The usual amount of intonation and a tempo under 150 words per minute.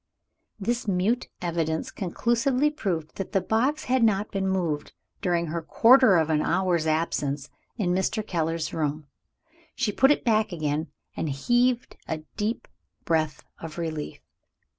No: wide, 5.7 semitones; average, 140 wpm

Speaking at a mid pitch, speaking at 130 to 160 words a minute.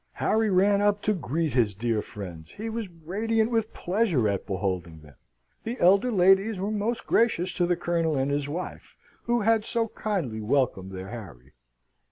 No: medium, 175 Hz; average, 175 wpm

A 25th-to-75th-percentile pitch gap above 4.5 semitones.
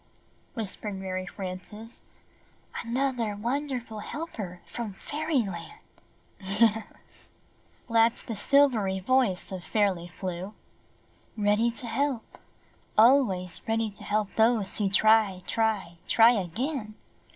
No: average, 3.7 semitones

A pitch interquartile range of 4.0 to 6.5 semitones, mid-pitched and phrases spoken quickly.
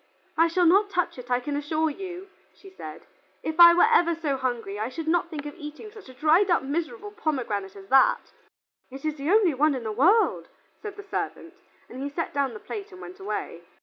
No: wide, 5.5 semitones; very high, 320 Hz; fast, 220 wpm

